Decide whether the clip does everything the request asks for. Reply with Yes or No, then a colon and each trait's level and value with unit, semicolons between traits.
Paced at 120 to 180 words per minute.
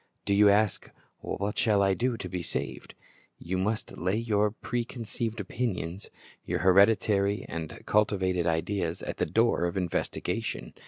Yes: average, 150 wpm